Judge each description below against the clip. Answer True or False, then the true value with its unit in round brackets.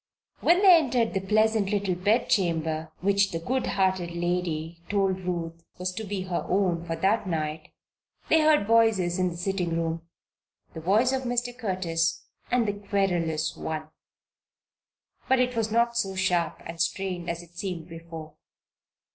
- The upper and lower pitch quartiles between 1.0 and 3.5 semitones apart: False (4.4 semitones)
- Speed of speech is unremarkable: True (165 wpm)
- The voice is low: False (185 Hz)